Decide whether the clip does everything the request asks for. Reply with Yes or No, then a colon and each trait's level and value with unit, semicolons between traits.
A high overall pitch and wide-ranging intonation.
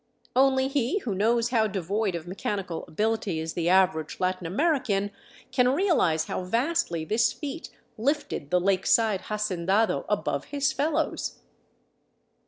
Yes: high, 210 Hz; wide, 6.3 semitones